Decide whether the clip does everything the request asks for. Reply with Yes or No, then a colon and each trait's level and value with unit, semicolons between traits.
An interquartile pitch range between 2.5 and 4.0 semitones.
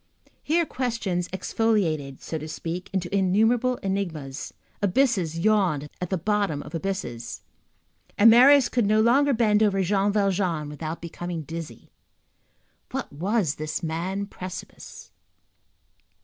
No: average, 4.7 semitones